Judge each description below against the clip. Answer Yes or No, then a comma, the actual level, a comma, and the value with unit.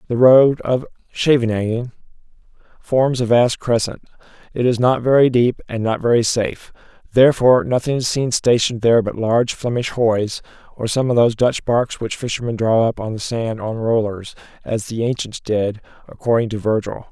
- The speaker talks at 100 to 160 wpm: No, average, 170 wpm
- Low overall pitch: Yes, low, 115 Hz